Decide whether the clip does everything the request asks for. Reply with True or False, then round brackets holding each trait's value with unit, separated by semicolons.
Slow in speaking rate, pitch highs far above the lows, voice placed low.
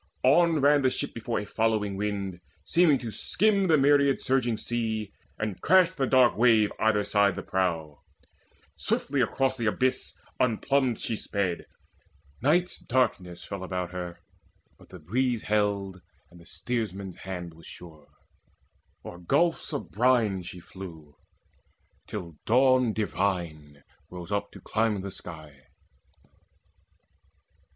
True (130 wpm; 6.0 semitones; 105 Hz)